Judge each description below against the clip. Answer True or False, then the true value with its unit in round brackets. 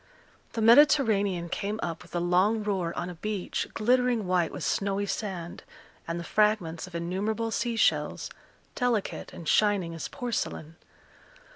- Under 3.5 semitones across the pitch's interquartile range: False (4.2 semitones)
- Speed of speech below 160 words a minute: True (145 wpm)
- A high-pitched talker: True (200 Hz)